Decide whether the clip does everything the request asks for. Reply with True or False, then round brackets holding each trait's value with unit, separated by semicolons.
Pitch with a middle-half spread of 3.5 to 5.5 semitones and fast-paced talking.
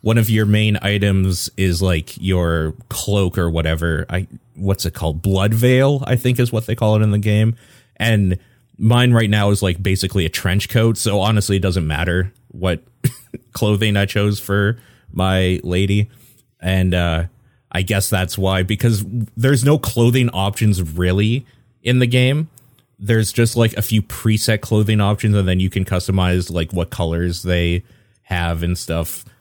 False (3.8 semitones; 170 wpm)